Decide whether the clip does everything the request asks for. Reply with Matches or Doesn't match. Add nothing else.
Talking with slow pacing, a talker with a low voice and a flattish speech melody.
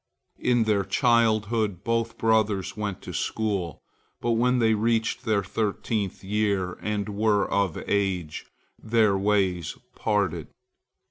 Matches